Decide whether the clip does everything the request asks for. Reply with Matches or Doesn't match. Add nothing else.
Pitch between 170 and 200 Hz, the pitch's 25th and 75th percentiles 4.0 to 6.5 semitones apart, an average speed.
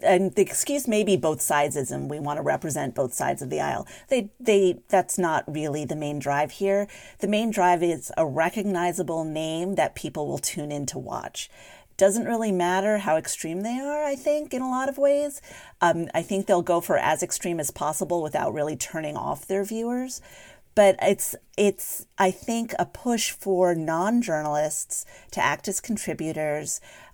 Matches